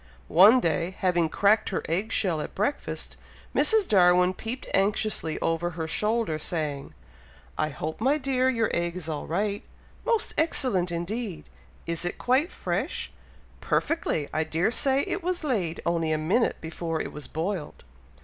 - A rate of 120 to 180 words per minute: Yes, average, 155 wpm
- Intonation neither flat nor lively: No, wide, 6.2 semitones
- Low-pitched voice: No, medium, 180 Hz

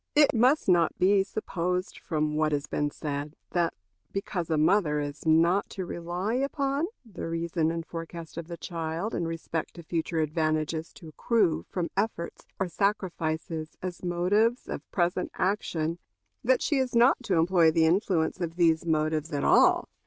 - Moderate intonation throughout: Yes, average, 3.3 semitones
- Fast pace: No, average, 165 wpm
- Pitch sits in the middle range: Yes, medium, 170 Hz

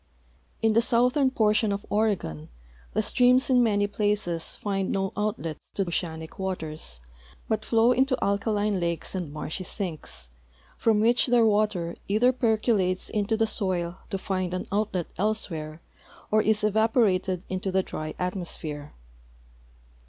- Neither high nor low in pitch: No, high, 200 Hz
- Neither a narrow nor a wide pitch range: Yes, average, 3.4 semitones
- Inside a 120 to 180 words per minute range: Yes, slow, 135 wpm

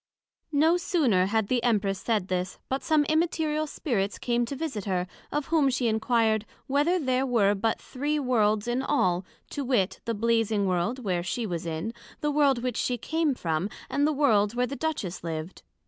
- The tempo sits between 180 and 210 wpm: Yes, average, 185 wpm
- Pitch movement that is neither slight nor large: No, wide, 6.0 semitones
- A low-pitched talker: No, high, 240 Hz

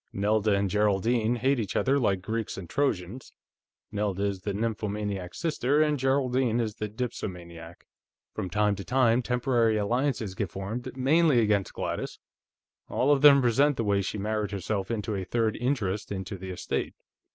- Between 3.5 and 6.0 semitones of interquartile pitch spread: Yes, average, 3.9 semitones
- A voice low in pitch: Yes, low, 110 Hz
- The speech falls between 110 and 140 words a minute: No, average, 165 wpm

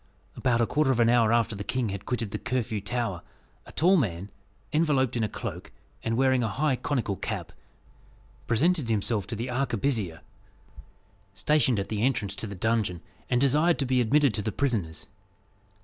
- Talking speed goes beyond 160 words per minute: Yes, average, 180 wpm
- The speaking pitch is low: Yes, low, 120 Hz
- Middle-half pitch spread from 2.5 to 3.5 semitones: No, average, 4.0 semitones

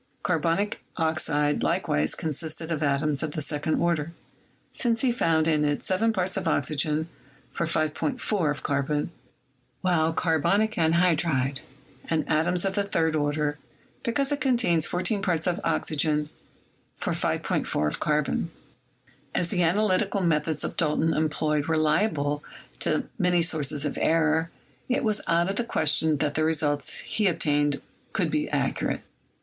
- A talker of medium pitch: Yes, medium, 160 Hz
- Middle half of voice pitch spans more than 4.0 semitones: No, average, 3.1 semitones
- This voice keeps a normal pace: Yes, average, 145 wpm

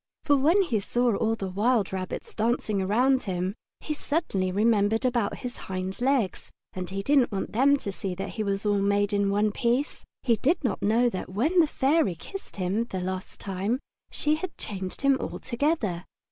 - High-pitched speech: Yes, high, 215 Hz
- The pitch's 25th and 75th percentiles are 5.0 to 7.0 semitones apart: Yes, average, 5.3 semitones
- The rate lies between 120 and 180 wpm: No, average, 190 wpm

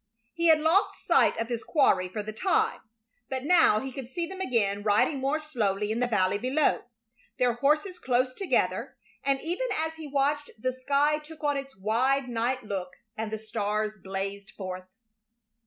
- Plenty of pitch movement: Yes, wide, 5.9 semitones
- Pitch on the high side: Yes, very high, 255 Hz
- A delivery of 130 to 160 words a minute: No, average, 175 wpm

